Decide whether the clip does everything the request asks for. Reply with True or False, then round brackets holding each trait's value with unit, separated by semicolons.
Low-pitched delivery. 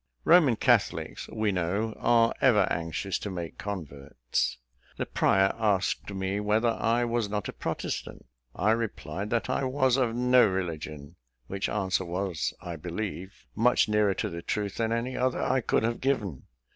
True (105 Hz)